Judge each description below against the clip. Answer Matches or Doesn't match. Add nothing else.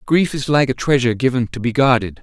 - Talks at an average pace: Doesn't match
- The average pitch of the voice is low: Matches